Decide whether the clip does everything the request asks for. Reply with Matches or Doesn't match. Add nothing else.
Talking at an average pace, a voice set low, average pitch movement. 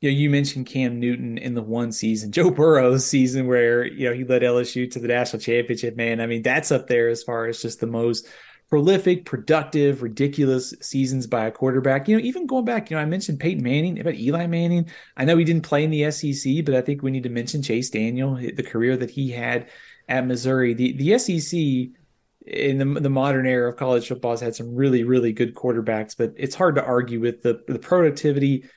Doesn't match